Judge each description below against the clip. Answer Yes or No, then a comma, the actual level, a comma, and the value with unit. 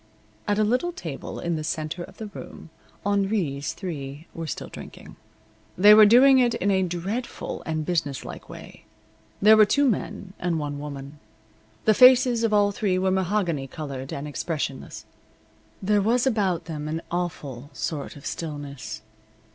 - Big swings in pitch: Yes, wide, 6.0 semitones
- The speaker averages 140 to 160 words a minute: Yes, average, 155 wpm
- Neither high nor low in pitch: Yes, medium, 175 Hz